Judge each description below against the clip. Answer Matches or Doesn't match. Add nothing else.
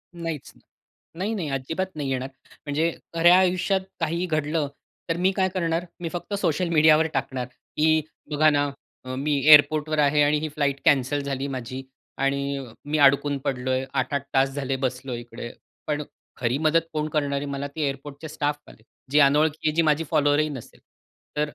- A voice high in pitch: Doesn't match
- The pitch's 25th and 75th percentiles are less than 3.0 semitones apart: Matches